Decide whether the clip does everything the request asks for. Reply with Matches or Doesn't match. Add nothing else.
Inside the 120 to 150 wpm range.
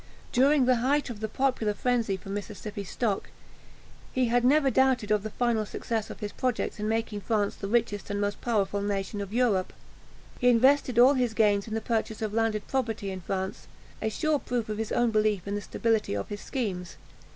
Doesn't match